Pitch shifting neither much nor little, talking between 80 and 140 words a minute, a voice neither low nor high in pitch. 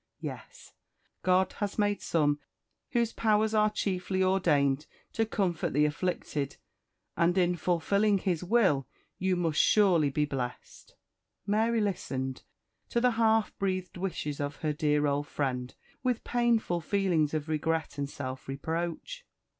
No: wide, 5.7 semitones; slow, 135 wpm; medium, 175 Hz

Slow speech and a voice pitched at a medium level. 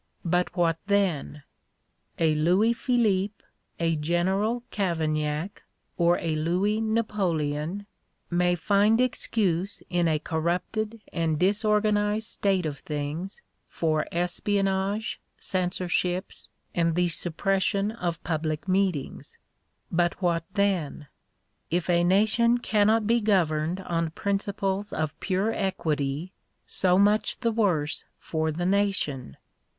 Yes: slow, 110 wpm; medium, 180 Hz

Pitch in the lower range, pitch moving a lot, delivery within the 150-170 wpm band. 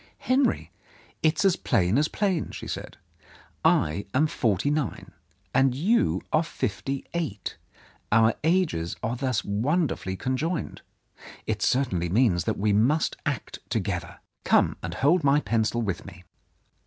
No: low, 130 Hz; wide, 7.4 semitones; slow, 135 wpm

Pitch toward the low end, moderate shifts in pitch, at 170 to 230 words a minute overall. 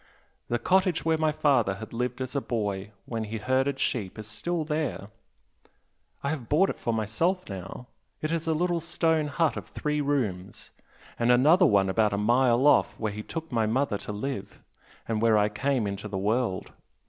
No: low, 125 Hz; wide, 6.2 semitones; average, 190 wpm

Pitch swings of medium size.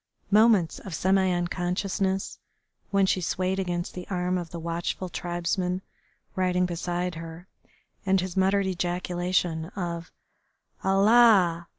No: narrow, 1.6 semitones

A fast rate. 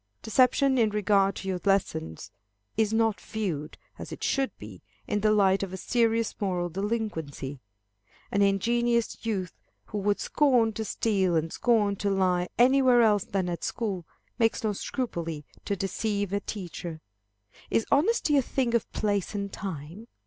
No: average, 155 wpm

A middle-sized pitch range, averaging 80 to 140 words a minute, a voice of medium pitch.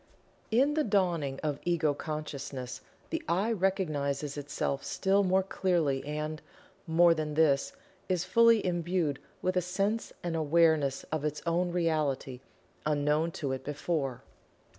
Yes: average, 4.0 semitones; slow, 135 wpm; medium, 160 Hz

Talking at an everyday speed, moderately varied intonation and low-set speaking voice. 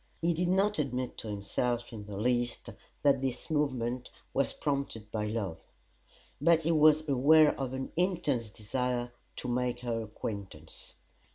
Yes: average, 150 wpm; average, 4.7 semitones; low, 125 Hz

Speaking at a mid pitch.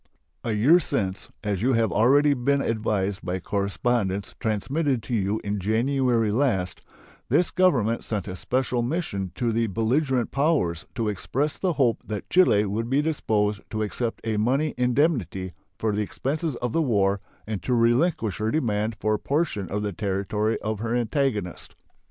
No: low, 115 Hz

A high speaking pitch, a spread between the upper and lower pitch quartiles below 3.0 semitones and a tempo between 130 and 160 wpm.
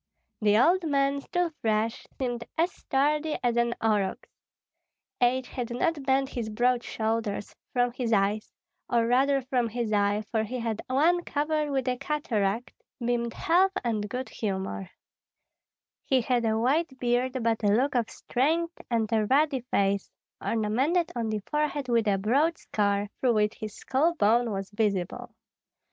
No: high, 240 Hz; average, 4.2 semitones; average, 155 wpm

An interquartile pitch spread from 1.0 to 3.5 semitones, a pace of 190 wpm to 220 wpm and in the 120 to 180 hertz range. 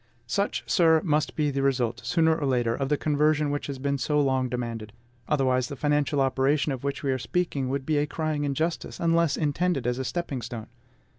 Yes: average, 2.9 semitones; fast, 205 wpm; medium, 140 Hz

